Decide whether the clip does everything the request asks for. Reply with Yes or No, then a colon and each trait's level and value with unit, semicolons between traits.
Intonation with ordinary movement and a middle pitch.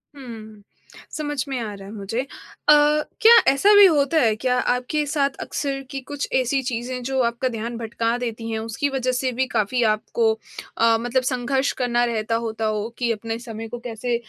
No: average, 3.0 semitones; high, 240 Hz